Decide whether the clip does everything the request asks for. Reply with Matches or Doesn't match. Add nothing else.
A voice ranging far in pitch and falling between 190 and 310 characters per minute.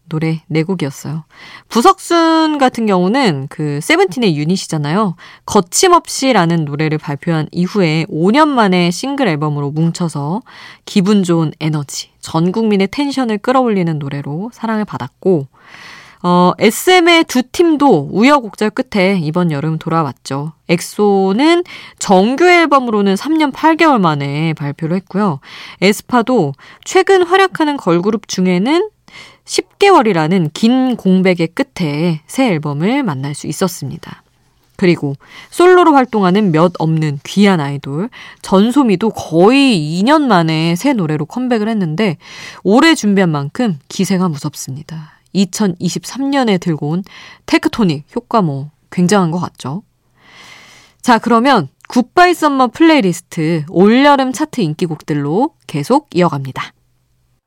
Matches